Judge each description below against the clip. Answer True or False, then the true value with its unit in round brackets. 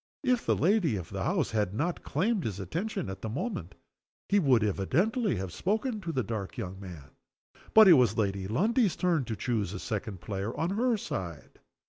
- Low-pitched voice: True (120 Hz)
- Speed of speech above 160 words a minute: True (190 wpm)